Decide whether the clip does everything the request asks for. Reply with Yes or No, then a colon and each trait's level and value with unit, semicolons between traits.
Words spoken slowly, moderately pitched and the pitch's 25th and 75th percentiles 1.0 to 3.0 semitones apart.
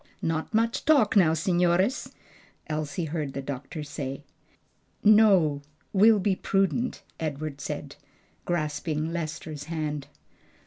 No: slow, 105 wpm; medium, 160 Hz; average, 4.4 semitones